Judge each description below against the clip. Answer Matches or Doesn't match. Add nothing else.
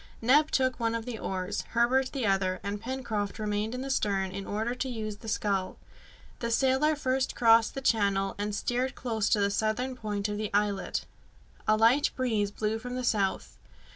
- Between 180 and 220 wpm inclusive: Matches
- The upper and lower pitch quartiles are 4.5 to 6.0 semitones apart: Doesn't match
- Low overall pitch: Doesn't match